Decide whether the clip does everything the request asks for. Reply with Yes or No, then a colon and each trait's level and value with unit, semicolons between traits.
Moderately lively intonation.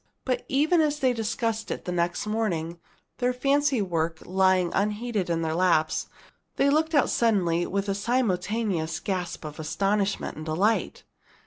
No: wide, 5.8 semitones